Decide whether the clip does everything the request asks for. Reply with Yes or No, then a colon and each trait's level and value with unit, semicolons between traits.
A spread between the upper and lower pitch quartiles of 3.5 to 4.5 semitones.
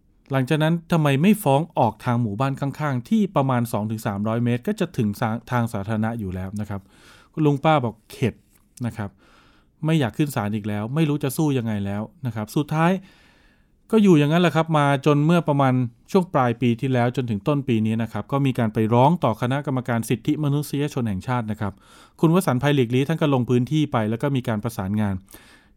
No: average, 5.1 semitones